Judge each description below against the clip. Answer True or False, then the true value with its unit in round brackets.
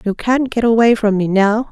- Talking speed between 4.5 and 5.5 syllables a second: True (5.0 syllables/s)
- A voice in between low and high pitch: False (220 Hz)